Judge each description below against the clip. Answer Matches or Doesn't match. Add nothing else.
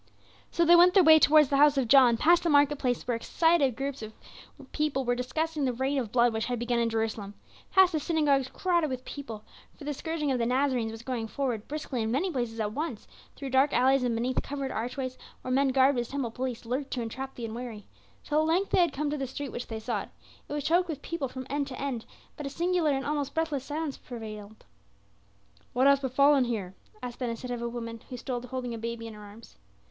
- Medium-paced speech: Doesn't match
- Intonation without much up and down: Doesn't match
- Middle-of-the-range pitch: Doesn't match